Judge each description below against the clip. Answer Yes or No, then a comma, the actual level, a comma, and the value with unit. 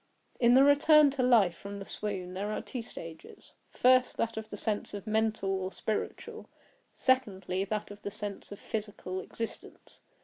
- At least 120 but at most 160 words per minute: No, average, 170 wpm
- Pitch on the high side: Yes, high, 210 Hz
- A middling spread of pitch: Yes, average, 3.4 semitones